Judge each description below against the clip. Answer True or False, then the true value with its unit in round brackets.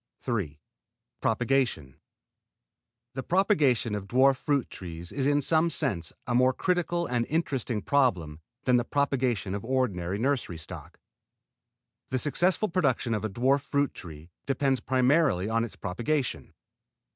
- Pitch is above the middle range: False (125 Hz)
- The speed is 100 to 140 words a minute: True (135 wpm)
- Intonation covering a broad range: True (5.7 semitones)